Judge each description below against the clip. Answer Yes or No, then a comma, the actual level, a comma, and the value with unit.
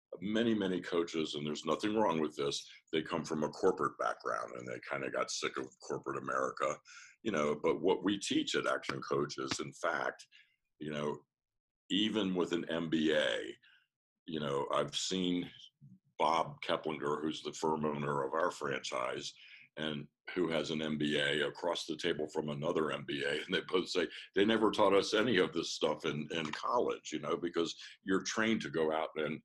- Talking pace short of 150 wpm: No, average, 180 wpm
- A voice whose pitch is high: No, very low, 80 Hz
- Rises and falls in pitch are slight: No, average, 3.1 semitones